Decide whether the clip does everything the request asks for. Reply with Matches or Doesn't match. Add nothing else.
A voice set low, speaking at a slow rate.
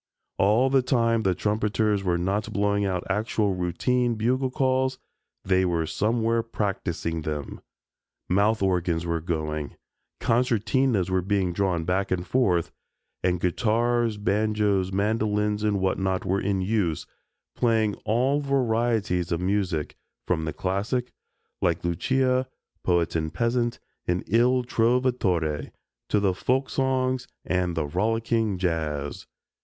Matches